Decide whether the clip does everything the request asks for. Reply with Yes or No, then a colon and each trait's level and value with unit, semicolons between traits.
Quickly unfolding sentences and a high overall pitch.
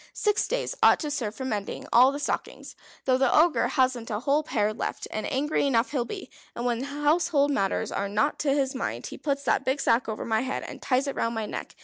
Yes: fast, 235 wpm; very high, 265 Hz